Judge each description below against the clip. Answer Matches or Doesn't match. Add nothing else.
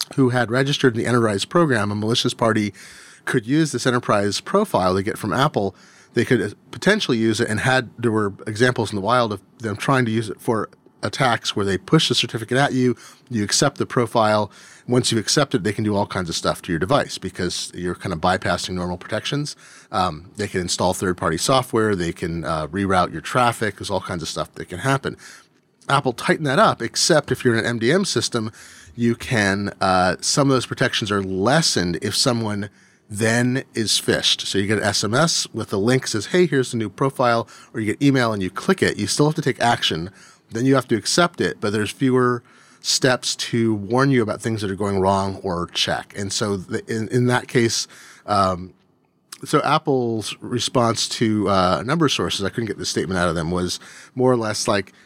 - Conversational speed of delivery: Doesn't match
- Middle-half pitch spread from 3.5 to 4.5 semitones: Matches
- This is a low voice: Matches